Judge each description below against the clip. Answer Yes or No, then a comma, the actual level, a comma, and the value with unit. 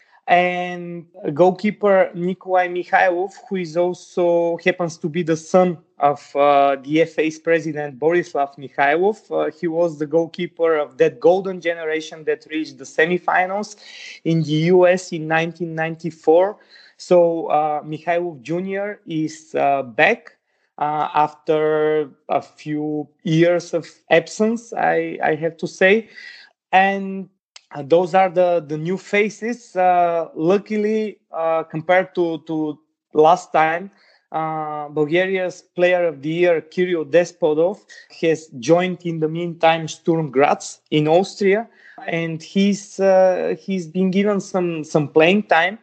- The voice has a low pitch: No, medium, 170 Hz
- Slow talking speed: Yes, slow, 130 wpm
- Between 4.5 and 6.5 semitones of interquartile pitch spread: No, average, 2.8 semitones